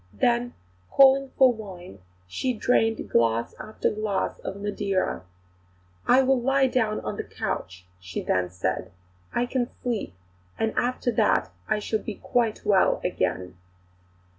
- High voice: Yes, high, 215 Hz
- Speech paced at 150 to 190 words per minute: No, average, 140 wpm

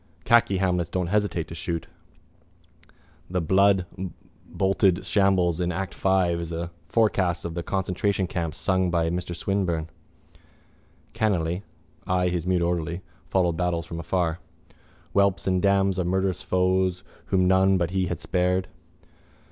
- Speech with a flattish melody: Yes, narrow, 1.8 semitones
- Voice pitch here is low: Yes, very low, 90 Hz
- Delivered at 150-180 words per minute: No, slow, 135 wpm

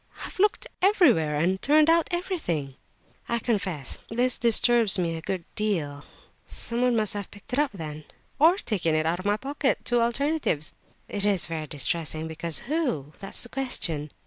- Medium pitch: No, high, 205 Hz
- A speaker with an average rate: Yes, average, 165 wpm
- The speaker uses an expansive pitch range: Yes, wide, 7.9 semitones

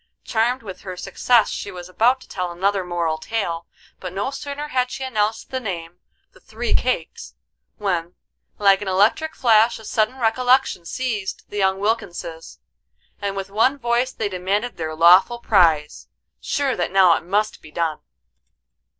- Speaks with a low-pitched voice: No, high, 205 Hz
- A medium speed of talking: Yes, average, 160 wpm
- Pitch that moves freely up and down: No, average, 5.0 semitones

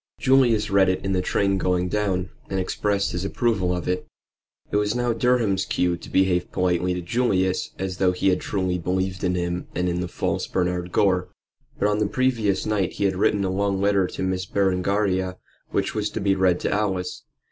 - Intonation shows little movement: Yes, narrow, 2.0 semitones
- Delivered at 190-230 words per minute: Yes, average, 200 wpm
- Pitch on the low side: Yes, very low, 95 Hz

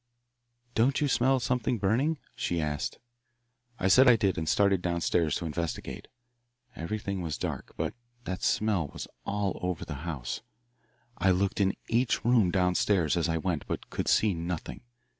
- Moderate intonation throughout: Yes, average, 4.6 semitones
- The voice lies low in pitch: Yes, very low, 95 Hz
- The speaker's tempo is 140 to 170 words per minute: Yes, average, 165 wpm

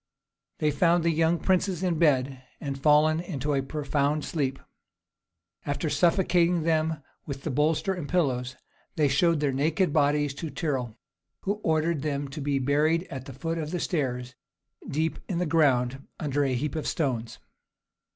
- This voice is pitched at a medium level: Yes, medium, 150 Hz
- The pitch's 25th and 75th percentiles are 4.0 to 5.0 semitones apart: No, average, 3.1 semitones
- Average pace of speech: Yes, average, 160 wpm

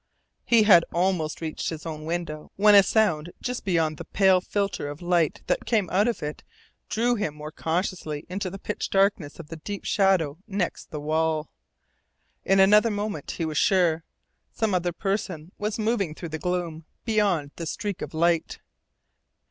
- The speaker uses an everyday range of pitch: Yes, average, 4.2 semitones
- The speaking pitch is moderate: Yes, medium, 175 Hz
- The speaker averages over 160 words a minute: Yes, average, 170 wpm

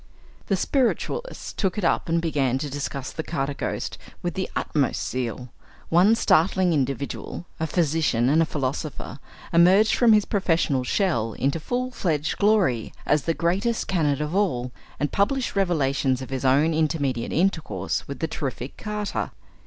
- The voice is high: No, medium, 160 Hz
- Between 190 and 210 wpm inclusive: No, average, 155 wpm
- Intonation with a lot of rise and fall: Yes, wide, 5.7 semitones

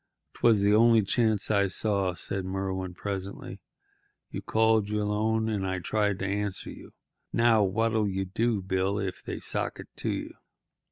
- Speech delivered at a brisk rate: No, average, 165 wpm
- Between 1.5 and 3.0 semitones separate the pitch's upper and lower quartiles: Yes, narrow, 2.4 semitones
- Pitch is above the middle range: No, low, 100 Hz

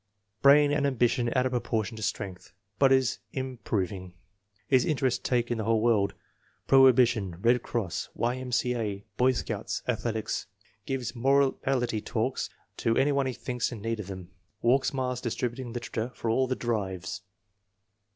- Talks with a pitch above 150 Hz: No, low, 120 Hz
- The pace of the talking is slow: No, average, 160 wpm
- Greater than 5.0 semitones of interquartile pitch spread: No, average, 3.2 semitones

